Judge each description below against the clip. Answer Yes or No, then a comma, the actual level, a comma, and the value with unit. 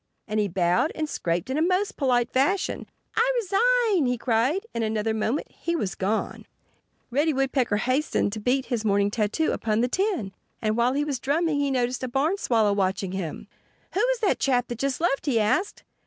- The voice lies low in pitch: No, very high, 255 Hz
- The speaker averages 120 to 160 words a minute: No, average, 195 wpm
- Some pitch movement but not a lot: No, wide, 6.5 semitones